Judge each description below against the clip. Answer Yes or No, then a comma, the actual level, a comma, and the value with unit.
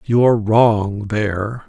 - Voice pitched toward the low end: Yes, low, 110 Hz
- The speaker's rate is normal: Yes, average, 145 wpm